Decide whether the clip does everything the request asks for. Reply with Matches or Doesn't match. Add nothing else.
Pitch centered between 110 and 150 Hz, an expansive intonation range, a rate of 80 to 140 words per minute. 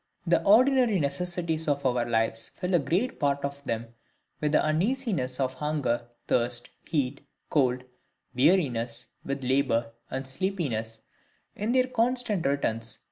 Matches